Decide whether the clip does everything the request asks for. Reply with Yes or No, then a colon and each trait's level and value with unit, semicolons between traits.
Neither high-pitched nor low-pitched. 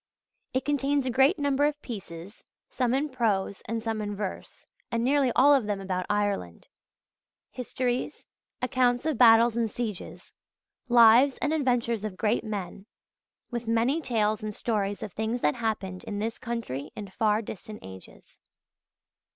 No: high, 230 Hz